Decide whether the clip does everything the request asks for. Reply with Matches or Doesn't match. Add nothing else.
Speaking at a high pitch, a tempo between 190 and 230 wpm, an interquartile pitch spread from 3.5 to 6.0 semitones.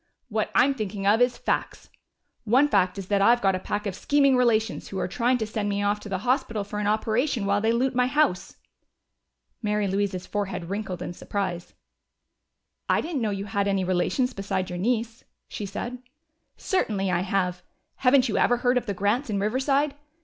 Matches